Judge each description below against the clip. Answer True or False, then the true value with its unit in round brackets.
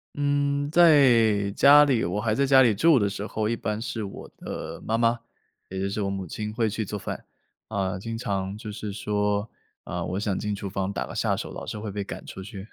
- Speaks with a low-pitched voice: True (105 Hz)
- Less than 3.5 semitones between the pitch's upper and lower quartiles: True (2.9 semitones)